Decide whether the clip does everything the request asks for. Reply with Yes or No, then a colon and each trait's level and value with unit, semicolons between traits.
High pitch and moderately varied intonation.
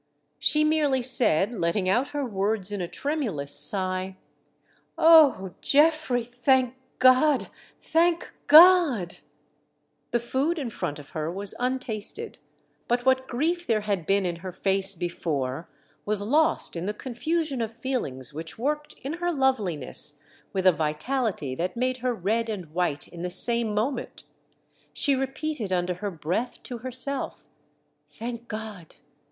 No: high, 230 Hz; wide, 6.5 semitones